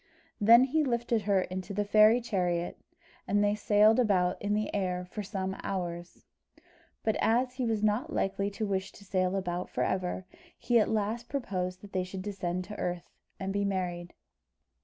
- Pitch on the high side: Yes, high, 200 Hz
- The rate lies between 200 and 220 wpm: No, average, 180 wpm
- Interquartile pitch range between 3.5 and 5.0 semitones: No, average, 2.8 semitones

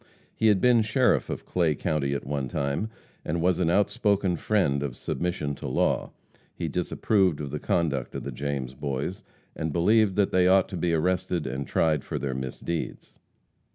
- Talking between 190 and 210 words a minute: No, average, 180 wpm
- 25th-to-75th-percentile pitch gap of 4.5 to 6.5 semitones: Yes, average, 5.2 semitones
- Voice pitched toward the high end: No, very low, 85 Hz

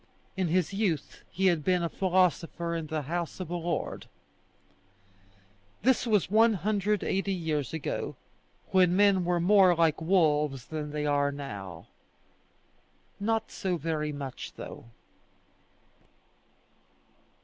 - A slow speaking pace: Yes, slow, 115 wpm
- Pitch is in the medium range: Yes, medium, 170 Hz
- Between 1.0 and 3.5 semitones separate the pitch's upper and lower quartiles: No, average, 4.0 semitones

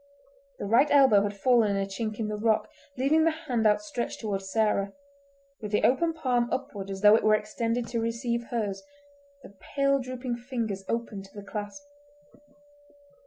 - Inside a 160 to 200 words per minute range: Yes, average, 170 wpm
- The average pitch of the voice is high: Yes, high, 230 Hz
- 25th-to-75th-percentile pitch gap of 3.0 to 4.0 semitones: Yes, average, 3.5 semitones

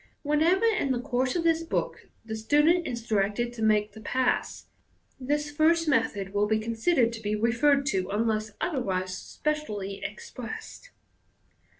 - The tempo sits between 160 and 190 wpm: No, average, 150 wpm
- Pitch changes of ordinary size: No, wide, 5.8 semitones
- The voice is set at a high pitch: Yes, high, 240 Hz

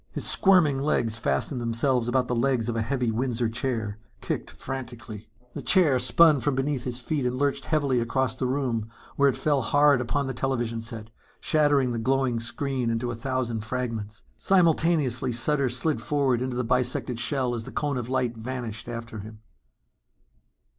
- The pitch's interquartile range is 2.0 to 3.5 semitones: Yes, average, 2.9 semitones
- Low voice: Yes, low, 125 Hz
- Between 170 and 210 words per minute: Yes, average, 175 wpm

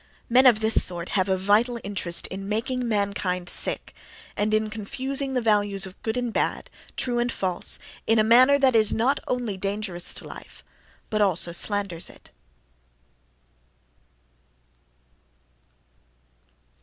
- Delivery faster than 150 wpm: No, slow, 135 wpm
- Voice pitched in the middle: No, high, 215 Hz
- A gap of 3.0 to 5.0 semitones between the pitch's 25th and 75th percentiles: Yes, average, 3.6 semitones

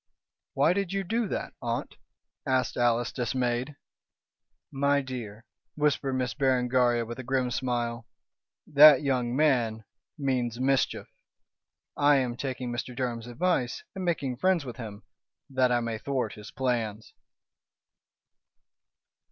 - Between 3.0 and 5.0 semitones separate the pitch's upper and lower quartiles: No, narrow, 2.6 semitones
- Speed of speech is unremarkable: No, slow, 125 wpm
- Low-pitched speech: Yes, low, 130 Hz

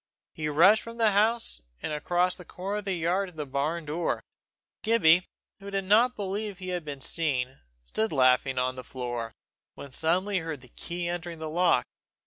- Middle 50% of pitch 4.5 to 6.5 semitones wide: Yes, wide, 5.5 semitones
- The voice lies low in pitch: No, medium, 170 Hz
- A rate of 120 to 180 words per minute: No, average, 190 wpm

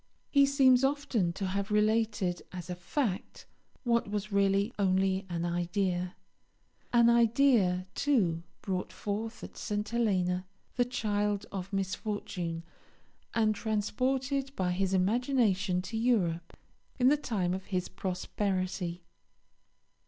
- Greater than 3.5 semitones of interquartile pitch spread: Yes, average, 4.3 semitones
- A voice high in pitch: Yes, high, 200 Hz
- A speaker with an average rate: No, slow, 120 wpm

